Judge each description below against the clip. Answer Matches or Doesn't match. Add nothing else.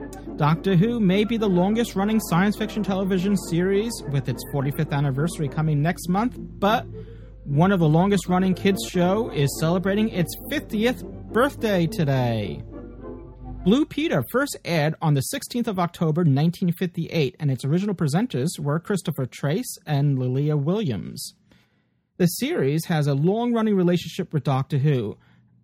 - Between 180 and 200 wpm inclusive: Doesn't match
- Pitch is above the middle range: Doesn't match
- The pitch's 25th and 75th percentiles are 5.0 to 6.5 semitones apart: Matches